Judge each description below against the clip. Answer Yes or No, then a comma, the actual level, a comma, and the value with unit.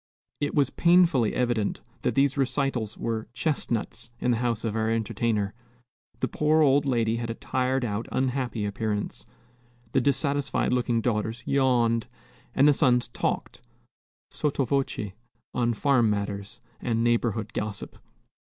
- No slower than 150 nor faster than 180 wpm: No, slow, 135 wpm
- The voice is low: Yes, low, 120 Hz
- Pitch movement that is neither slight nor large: Yes, average, 3.3 semitones